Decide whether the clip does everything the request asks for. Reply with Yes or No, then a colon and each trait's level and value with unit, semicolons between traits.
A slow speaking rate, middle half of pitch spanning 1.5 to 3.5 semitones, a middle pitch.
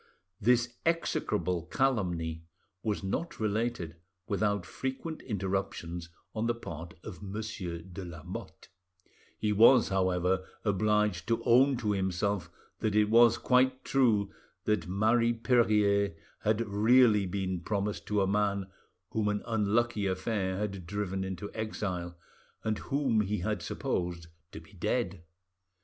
No: slow, 130 wpm; average, 3.2 semitones; low, 105 Hz